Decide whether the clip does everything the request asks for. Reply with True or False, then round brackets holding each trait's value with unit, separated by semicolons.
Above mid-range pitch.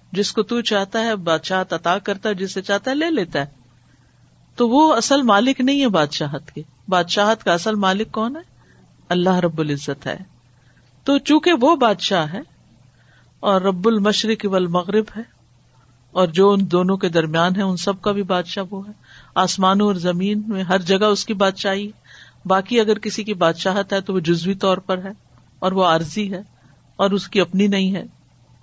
True (195 Hz)